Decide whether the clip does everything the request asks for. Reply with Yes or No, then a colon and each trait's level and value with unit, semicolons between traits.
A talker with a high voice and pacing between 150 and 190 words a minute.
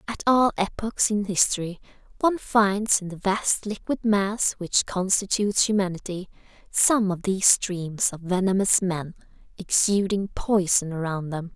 No: high, 195 Hz; slow, 135 wpm